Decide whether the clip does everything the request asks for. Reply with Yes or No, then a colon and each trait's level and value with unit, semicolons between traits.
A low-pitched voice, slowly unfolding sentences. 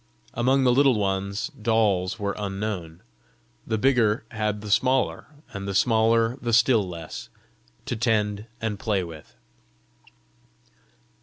Yes: low, 105 Hz; slow, 125 wpm